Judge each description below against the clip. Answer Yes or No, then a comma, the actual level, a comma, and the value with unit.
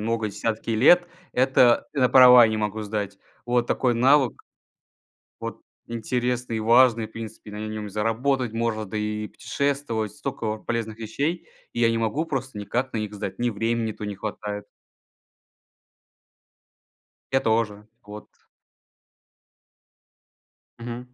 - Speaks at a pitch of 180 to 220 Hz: No, low, 115 Hz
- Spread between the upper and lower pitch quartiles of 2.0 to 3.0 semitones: Yes, average, 2.7 semitones